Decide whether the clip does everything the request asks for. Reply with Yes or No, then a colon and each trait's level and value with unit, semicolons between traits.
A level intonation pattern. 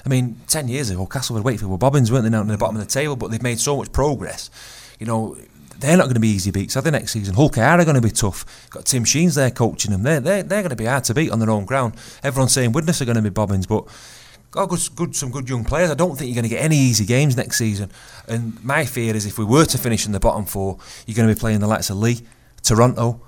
No: average, 4.1 semitones